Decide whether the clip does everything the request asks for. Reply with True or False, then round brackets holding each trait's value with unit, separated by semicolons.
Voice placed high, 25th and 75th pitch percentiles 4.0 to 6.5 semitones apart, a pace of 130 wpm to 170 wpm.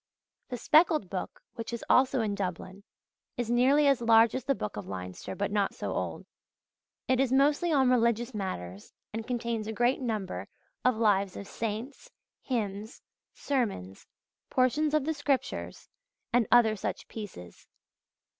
True (230 Hz; 4.4 semitones; 150 wpm)